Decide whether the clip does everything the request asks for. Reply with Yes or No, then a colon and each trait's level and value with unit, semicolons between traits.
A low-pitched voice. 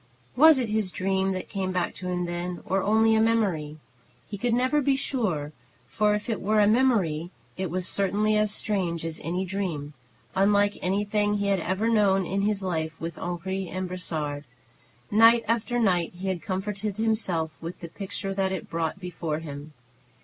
No: high, 195 Hz